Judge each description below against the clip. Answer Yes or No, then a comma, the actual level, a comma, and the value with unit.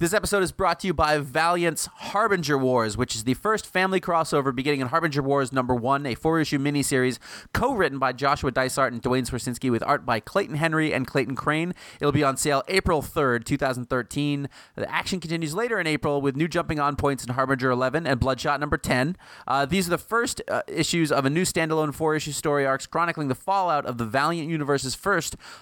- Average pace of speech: No, fast, 210 wpm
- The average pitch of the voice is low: No, medium, 145 Hz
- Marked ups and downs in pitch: No, average, 3.6 semitones